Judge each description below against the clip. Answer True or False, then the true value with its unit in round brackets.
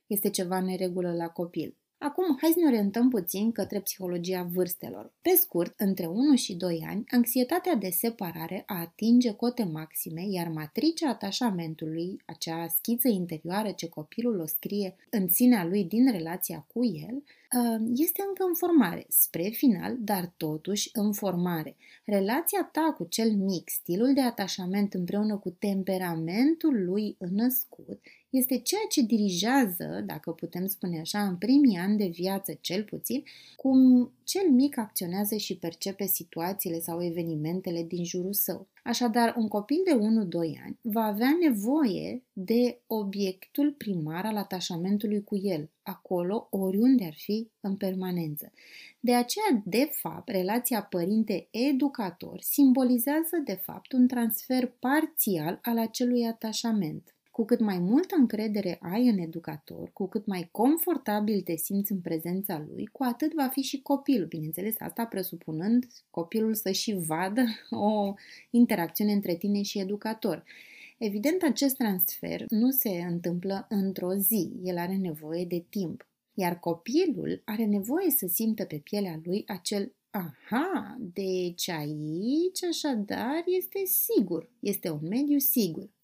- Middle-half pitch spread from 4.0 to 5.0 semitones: False (5.4 semitones)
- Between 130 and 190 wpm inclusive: True (140 wpm)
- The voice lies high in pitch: True (205 Hz)